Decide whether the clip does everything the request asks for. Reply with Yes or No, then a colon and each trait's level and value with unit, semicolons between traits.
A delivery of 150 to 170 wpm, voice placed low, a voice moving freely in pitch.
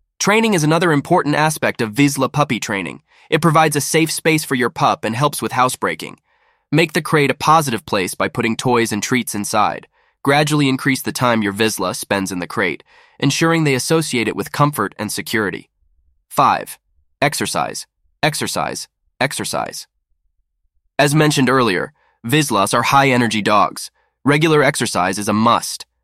Yes: average, 155 wpm; low, 125 Hz; wide, 6.2 semitones